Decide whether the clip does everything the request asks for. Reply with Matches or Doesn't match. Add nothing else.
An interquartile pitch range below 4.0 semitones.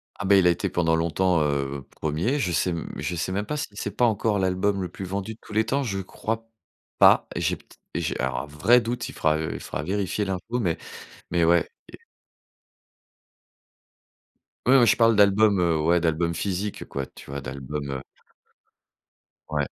Doesn't match